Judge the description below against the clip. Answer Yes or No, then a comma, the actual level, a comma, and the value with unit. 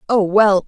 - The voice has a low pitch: No, high, 200 Hz